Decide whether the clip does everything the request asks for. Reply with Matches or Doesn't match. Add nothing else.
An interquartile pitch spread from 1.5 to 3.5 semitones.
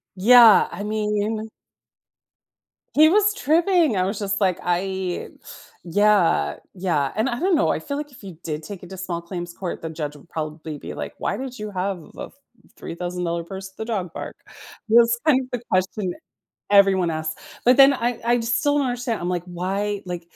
Doesn't match